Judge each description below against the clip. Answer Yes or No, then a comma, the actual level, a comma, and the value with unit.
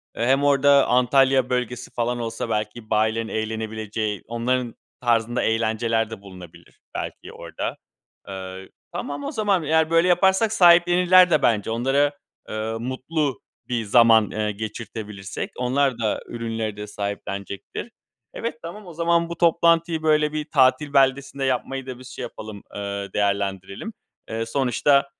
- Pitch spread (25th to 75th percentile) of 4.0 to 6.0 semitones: Yes, average, 4.8 semitones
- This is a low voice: Yes, low, 125 Hz